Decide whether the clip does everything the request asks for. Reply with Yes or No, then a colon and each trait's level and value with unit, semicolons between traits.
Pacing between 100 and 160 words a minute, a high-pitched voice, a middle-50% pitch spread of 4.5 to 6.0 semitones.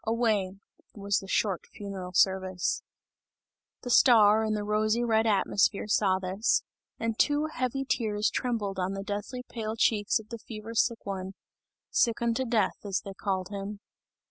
No: average, 155 wpm; high, 210 Hz; average, 2.7 semitones